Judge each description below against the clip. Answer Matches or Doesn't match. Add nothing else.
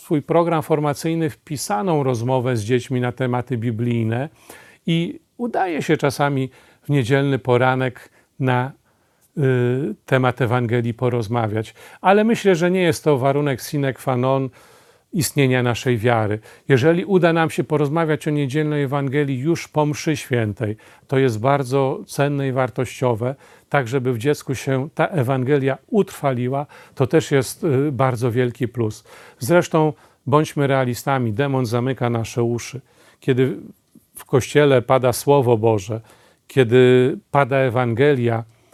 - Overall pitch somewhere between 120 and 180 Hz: Matches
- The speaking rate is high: Doesn't match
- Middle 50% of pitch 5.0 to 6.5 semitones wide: Doesn't match